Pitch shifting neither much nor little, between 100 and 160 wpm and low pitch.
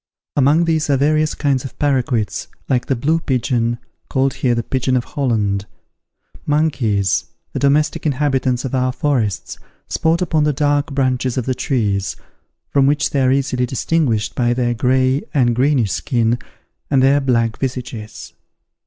Yes: average, 3.0 semitones; average, 155 wpm; low, 130 Hz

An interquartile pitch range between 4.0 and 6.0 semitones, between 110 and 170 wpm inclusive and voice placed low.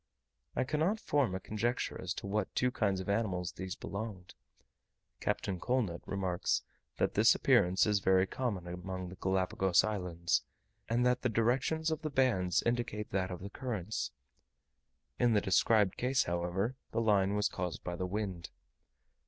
Yes: average, 4.5 semitones; average, 160 wpm; low, 100 Hz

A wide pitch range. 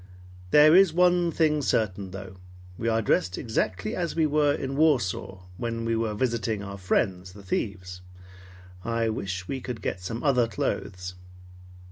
Yes: wide, 6.9 semitones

